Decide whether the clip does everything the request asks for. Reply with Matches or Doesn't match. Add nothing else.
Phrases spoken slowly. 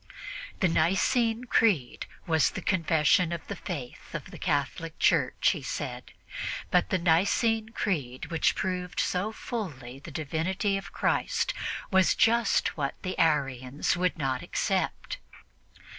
Matches